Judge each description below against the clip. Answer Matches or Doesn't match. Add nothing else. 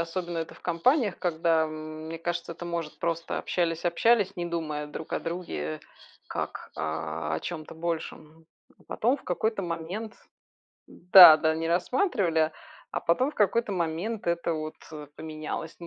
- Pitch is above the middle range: Doesn't match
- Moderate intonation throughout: Doesn't match